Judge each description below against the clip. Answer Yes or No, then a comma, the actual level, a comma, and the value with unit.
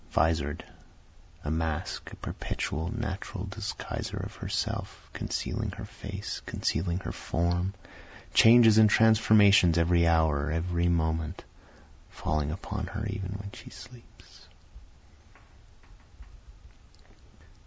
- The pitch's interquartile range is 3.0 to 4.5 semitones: Yes, average, 4.1 semitones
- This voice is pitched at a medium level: No, very low, 90 Hz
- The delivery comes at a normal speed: No, slow, 100 wpm